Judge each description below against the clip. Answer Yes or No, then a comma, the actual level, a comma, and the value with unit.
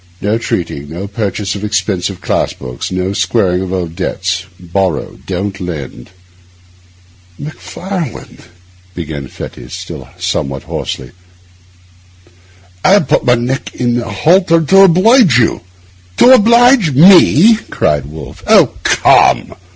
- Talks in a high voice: No, low, 100 Hz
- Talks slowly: Yes, slow, 120 wpm